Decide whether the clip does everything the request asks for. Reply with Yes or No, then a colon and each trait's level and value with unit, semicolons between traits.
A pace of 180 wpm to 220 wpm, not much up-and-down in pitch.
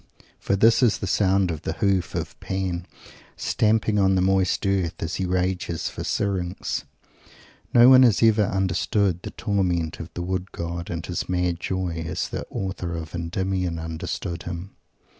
No: average, 165 wpm; narrow, 2.2 semitones